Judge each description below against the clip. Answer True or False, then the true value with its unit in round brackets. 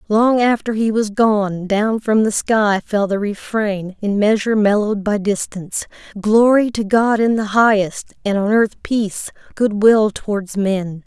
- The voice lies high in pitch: True (210 Hz)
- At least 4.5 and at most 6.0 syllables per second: False (4.3 syllables/s)